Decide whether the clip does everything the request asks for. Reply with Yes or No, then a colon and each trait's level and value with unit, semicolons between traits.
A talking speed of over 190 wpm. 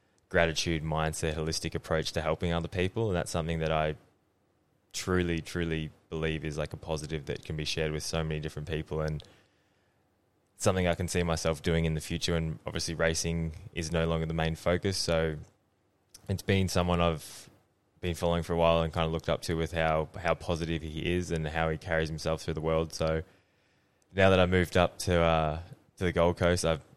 Yes: average, 200 wpm